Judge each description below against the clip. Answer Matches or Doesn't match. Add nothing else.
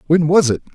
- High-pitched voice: Doesn't match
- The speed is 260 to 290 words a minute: Doesn't match